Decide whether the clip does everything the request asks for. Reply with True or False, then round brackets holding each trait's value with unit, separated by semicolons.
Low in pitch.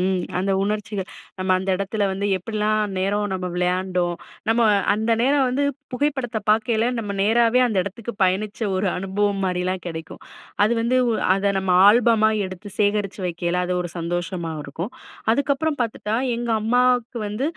False (205 Hz)